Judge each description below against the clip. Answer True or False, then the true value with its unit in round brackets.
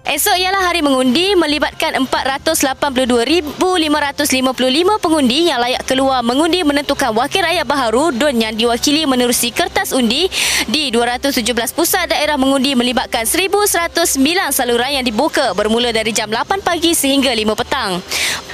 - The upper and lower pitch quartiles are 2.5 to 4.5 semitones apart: False (5.2 semitones)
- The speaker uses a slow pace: False (125 wpm)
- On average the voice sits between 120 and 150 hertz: False (280 Hz)